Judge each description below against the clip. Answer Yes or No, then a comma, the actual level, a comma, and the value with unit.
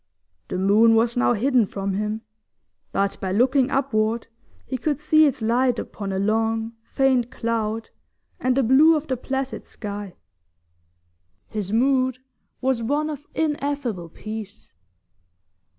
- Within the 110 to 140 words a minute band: Yes, slow, 135 wpm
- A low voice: No, high, 235 Hz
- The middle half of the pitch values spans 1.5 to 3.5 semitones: No, average, 3.9 semitones